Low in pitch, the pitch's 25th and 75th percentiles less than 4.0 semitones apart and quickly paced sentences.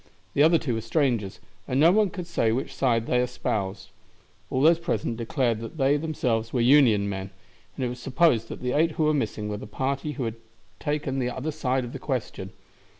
No: low, 130 Hz; average, 4.5 semitones; fast, 210 wpm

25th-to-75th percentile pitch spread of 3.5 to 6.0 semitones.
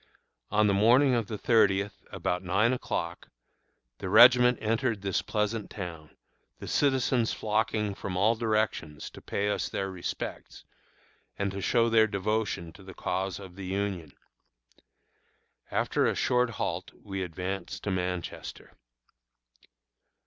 No: average, 3.1 semitones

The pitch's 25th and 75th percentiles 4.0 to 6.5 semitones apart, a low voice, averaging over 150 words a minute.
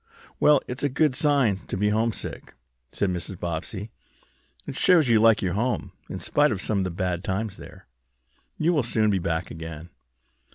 Yes: wide, 5.6 semitones; low, 105 Hz; average, 170 wpm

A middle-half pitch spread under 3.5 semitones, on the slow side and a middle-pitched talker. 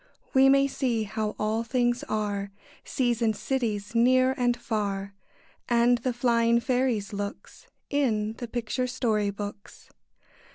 No: average, 2.9 semitones; slow, 130 wpm; high, 235 Hz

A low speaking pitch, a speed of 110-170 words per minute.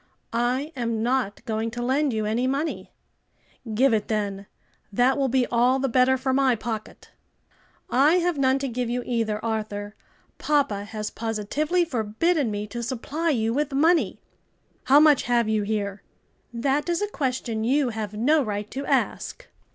No: high, 245 Hz; average, 165 wpm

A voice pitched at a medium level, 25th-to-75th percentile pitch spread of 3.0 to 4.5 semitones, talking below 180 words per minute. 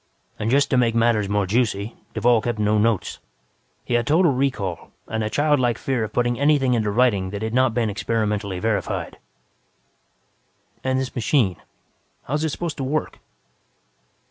No: low, 115 Hz; average, 3.6 semitones; average, 165 wpm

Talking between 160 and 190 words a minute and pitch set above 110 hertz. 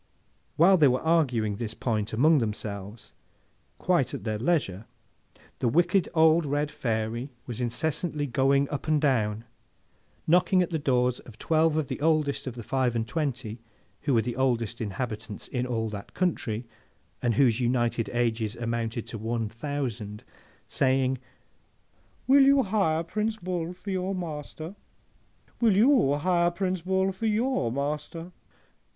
No: average, 145 wpm; low, 135 Hz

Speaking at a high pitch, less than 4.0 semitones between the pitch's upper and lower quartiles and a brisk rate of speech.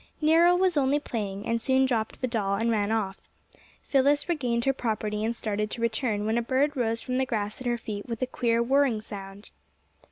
Yes: high, 230 Hz; average, 3.6 semitones; fast, 210 wpm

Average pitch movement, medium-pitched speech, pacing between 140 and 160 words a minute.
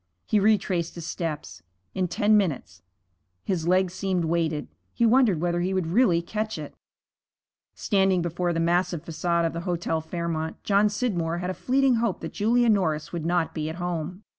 No: average, 3.3 semitones; medium, 175 Hz; average, 175 wpm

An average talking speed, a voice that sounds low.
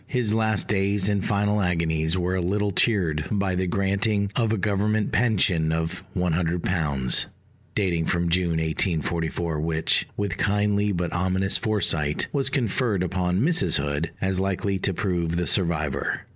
Yes: average, 145 wpm; very low, 95 Hz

